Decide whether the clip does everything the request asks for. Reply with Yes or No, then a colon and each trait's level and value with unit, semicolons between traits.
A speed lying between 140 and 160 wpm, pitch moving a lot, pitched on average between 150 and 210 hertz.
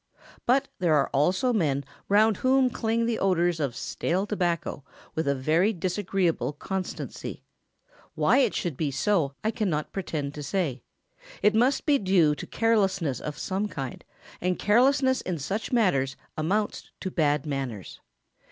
Yes: average, 150 wpm; wide, 6.2 semitones; medium, 185 Hz